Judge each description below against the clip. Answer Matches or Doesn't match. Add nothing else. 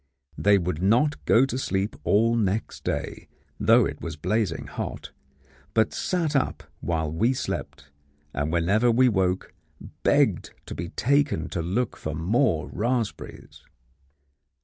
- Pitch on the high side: Doesn't match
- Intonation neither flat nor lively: Doesn't match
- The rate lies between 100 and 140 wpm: Matches